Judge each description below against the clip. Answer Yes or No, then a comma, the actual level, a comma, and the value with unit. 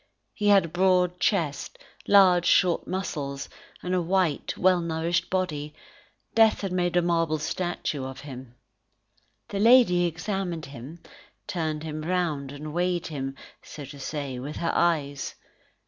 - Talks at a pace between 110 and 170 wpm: Yes, average, 145 wpm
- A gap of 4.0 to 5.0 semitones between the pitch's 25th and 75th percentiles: No, average, 3.6 semitones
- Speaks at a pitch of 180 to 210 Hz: No, medium, 170 Hz